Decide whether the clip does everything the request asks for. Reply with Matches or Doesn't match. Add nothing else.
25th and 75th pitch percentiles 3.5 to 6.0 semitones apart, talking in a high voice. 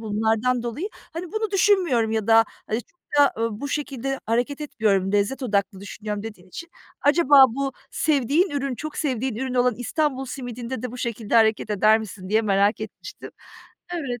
Matches